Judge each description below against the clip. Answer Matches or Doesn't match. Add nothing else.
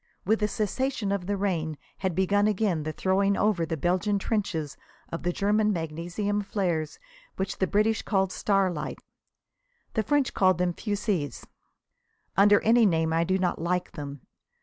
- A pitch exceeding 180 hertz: Matches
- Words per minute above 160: Doesn't match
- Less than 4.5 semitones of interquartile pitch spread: Matches